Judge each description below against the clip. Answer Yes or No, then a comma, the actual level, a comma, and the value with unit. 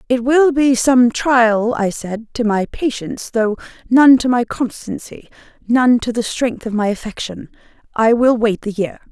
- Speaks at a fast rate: No, average, 170 wpm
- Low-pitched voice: No, high, 235 Hz